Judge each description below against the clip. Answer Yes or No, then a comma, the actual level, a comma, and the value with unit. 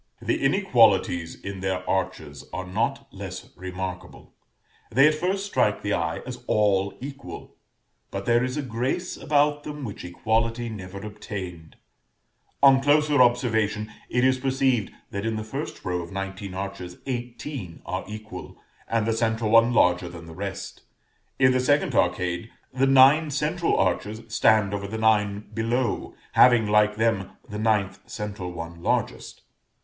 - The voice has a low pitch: Yes, low, 110 Hz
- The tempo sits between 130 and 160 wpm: Yes, average, 150 wpm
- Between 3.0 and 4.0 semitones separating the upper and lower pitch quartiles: No, average, 4.9 semitones